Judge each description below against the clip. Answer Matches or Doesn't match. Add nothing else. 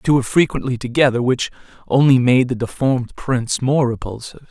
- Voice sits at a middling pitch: Doesn't match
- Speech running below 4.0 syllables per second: Doesn't match